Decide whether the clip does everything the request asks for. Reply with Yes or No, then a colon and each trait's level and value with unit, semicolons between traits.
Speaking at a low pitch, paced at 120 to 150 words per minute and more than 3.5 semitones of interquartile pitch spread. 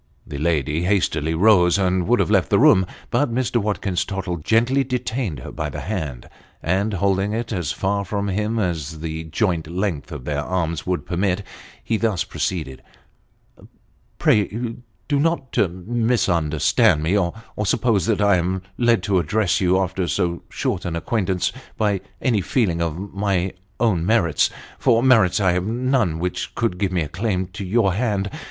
No: very low, 95 Hz; average, 170 wpm; average, 4.1 semitones